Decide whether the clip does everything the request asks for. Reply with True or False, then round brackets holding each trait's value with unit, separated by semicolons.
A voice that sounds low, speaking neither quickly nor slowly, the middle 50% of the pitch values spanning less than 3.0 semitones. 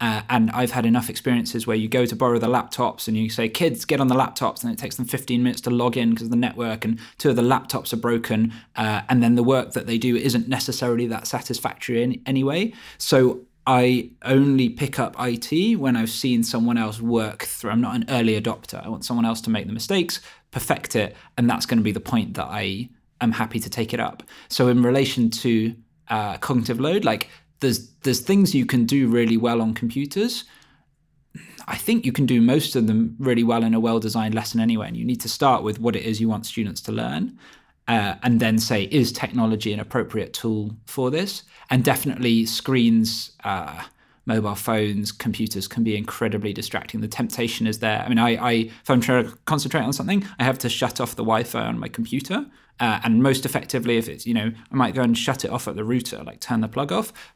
False (120 Hz; 225 wpm; 2.4 semitones)